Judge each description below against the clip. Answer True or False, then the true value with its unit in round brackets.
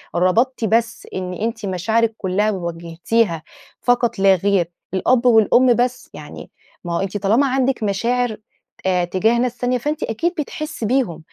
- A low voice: False (220 Hz)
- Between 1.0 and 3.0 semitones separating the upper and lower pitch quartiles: False (4.8 semitones)